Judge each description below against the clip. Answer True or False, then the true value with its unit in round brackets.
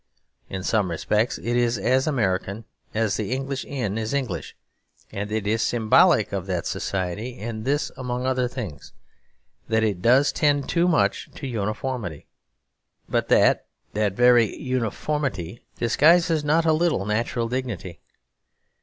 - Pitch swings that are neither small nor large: True (4.1 semitones)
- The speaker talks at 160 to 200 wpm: False (140 wpm)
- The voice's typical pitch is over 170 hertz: False (115 Hz)